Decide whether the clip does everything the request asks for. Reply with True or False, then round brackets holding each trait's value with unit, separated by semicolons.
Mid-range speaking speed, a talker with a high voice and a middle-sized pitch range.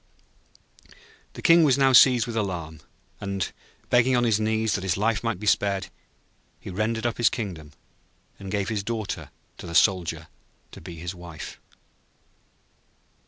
False (155 wpm; 105 Hz; 4.1 semitones)